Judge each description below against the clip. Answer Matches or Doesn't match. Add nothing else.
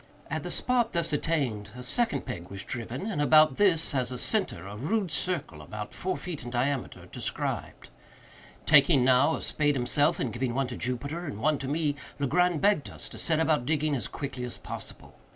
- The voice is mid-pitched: Matches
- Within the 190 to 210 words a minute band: Matches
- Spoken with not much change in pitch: Doesn't match